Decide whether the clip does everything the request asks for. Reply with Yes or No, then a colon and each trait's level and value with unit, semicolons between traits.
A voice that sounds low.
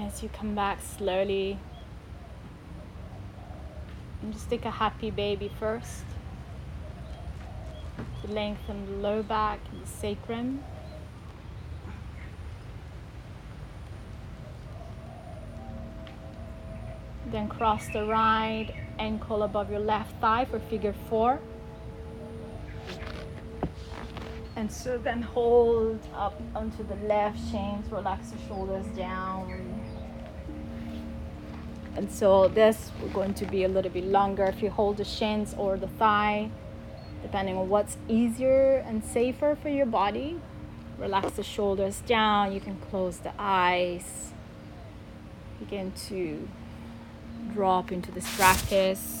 No: high, 195 Hz